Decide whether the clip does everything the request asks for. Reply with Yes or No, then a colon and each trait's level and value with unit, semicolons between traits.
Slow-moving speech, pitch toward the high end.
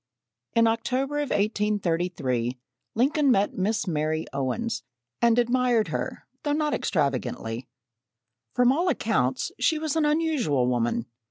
Yes: slow, 120 wpm; high, 225 Hz